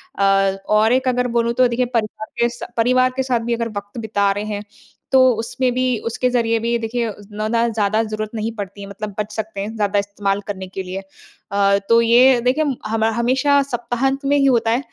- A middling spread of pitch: Yes, average, 3.2 semitones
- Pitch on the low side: No, high, 225 Hz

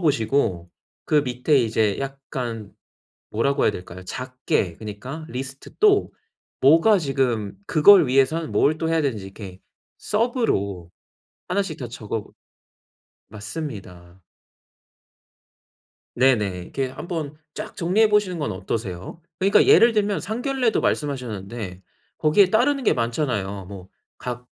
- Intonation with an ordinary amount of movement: No, wide, 7.9 semitones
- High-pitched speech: No, low, 130 Hz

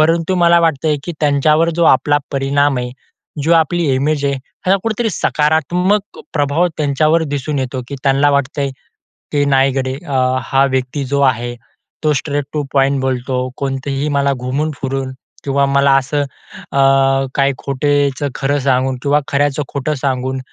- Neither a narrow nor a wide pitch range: No, narrow, 2.2 semitones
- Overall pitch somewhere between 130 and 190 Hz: Yes, medium, 140 Hz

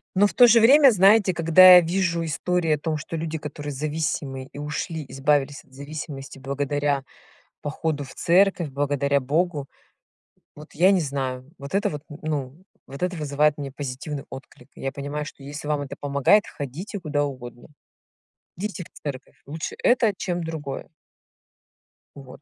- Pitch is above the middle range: No, medium, 150 Hz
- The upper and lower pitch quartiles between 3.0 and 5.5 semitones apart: Yes, average, 3.5 semitones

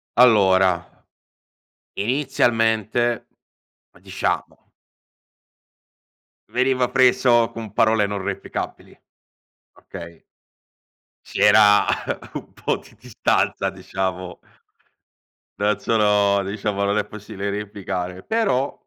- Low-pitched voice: Yes, low, 105 Hz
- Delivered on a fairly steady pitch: No, average, 3.3 semitones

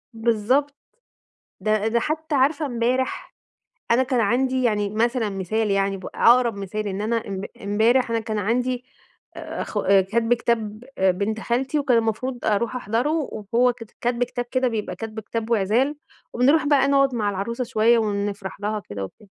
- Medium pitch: No, high, 230 Hz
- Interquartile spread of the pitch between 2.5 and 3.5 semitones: Yes, average, 3.2 semitones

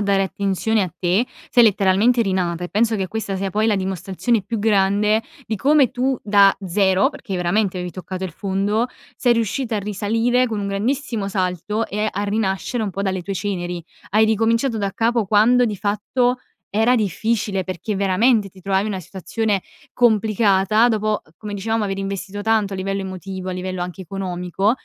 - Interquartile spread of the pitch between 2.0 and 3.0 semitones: Yes, average, 2.7 semitones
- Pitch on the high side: Yes, high, 200 Hz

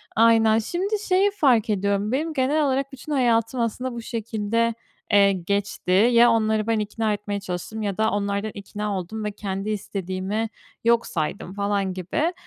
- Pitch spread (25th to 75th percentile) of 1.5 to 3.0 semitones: Yes, average, 2.7 semitones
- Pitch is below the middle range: No, high, 215 Hz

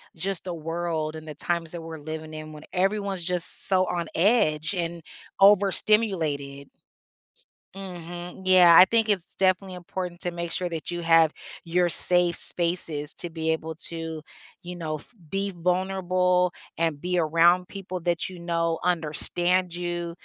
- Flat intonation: Yes, narrow, 2.0 semitones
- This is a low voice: No, medium, 175 Hz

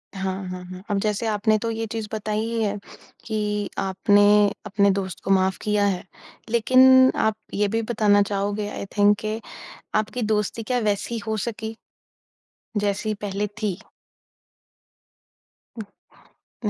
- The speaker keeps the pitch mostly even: Yes, narrow, 1.7 semitones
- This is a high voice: Yes, high, 210 Hz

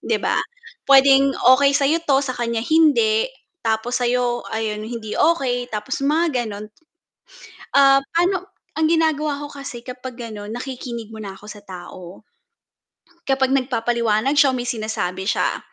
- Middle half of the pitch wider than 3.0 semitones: Yes, average, 4.2 semitones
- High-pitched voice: Yes, very high, 255 Hz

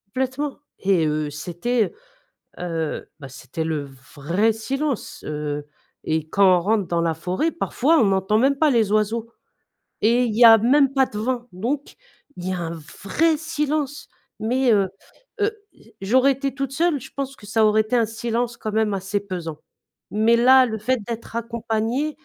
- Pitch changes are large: Yes, wide, 5.7 semitones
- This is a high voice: Yes, high, 225 Hz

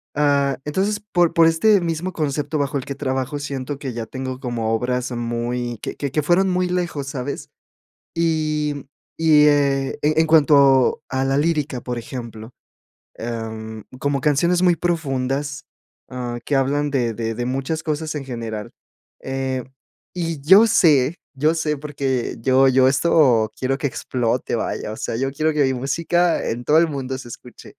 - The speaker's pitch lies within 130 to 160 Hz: Yes, medium, 140 Hz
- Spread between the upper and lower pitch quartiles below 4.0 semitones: Yes, average, 3.6 semitones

